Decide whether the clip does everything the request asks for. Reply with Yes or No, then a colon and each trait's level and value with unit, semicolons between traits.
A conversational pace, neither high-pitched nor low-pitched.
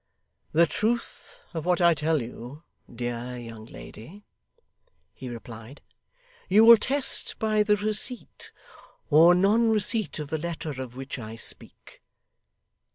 No: slow, 130 wpm; medium, 160 Hz